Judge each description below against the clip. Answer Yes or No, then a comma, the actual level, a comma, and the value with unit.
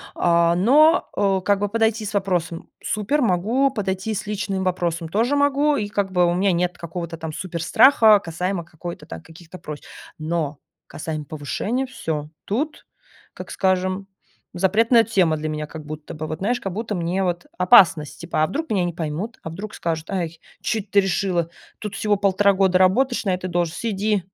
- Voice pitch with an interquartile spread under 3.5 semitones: No, average, 3.8 semitones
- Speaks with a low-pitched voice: No, medium, 185 Hz